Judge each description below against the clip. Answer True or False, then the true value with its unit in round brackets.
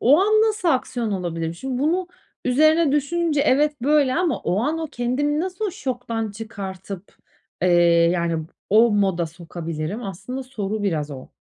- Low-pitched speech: False (245 Hz)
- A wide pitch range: True (8.0 semitones)